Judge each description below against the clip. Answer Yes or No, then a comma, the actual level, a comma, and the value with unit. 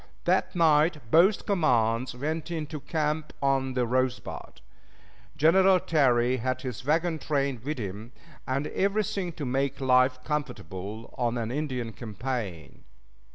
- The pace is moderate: No, slow, 125 wpm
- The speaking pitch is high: No, low, 135 Hz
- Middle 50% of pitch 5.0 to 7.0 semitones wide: No, average, 4.2 semitones